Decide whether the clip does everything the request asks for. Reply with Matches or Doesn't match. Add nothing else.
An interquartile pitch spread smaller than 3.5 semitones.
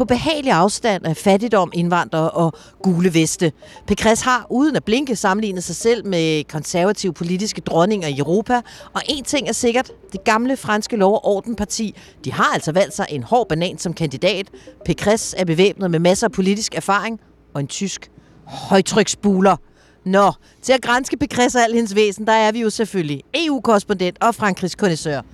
Doesn't match